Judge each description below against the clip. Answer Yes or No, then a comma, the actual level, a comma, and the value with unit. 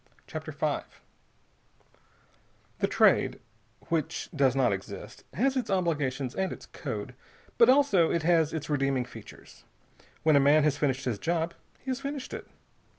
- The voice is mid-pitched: Yes, medium, 155 Hz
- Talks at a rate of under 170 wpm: Yes, average, 150 wpm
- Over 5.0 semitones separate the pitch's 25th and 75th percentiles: Yes, wide, 5.6 semitones